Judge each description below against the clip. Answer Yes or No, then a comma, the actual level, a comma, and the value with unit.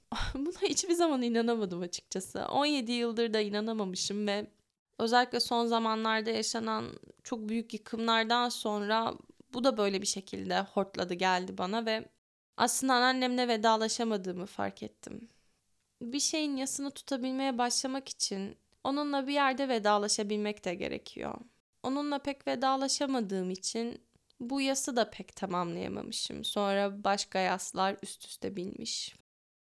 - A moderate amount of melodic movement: Yes, average, 4.7 semitones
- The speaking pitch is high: Yes, high, 230 Hz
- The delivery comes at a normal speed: Yes, average, 120 wpm